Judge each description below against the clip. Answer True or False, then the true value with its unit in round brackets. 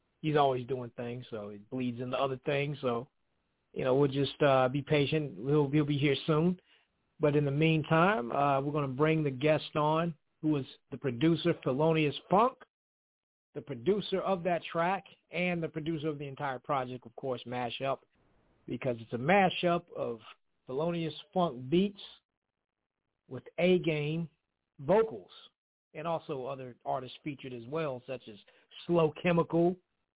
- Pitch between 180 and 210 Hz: False (150 Hz)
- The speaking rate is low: False (155 wpm)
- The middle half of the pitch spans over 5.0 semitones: False (3.8 semitones)